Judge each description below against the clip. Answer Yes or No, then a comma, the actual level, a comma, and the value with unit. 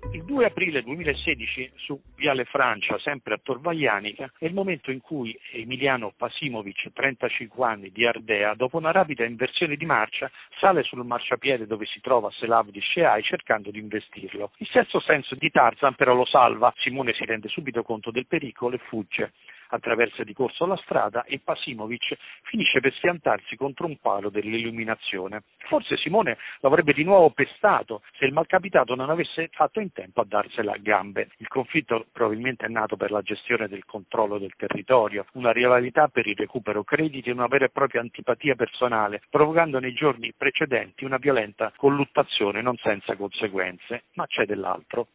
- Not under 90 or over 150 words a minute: No, average, 165 wpm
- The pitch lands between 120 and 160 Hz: Yes, low, 125 Hz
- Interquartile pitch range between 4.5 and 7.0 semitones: No, average, 4.1 semitones